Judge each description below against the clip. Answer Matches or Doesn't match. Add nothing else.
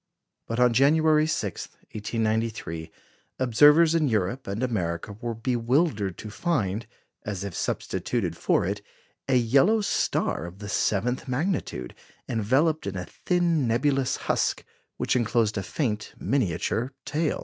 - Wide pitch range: Matches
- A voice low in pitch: Matches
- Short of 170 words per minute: Matches